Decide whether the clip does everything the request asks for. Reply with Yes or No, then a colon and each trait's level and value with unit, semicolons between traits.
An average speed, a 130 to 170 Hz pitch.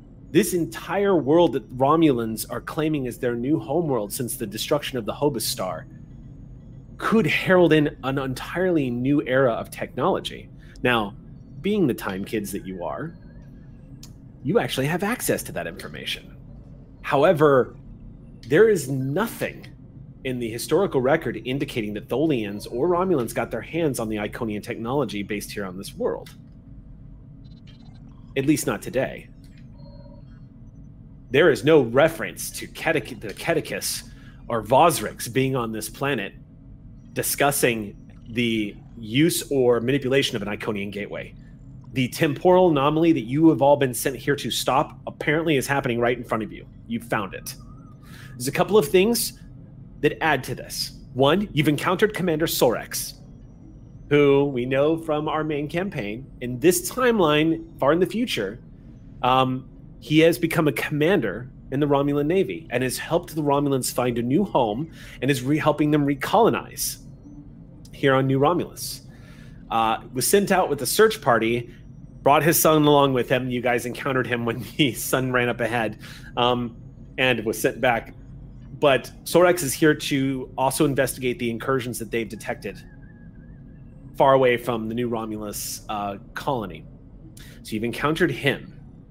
Yes: average, 155 wpm; low, 135 Hz